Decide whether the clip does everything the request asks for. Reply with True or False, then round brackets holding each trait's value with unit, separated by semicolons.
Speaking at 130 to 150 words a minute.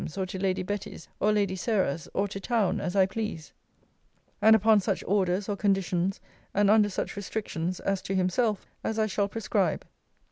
False (180 wpm)